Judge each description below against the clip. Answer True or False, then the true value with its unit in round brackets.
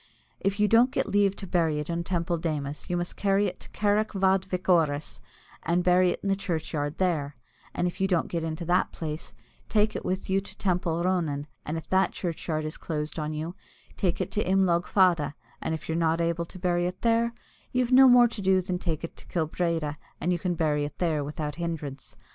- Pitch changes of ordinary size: True (3.1 semitones)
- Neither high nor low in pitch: True (175 Hz)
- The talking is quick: True (230 wpm)